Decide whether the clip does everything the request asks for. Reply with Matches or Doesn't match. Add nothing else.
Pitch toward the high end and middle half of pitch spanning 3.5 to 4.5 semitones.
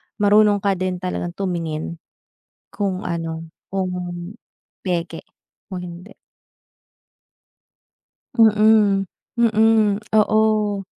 Doesn't match